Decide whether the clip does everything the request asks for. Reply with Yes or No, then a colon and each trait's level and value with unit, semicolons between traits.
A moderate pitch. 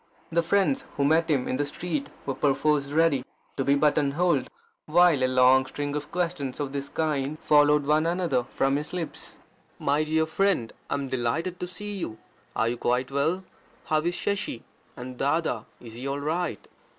Yes: medium, 145 Hz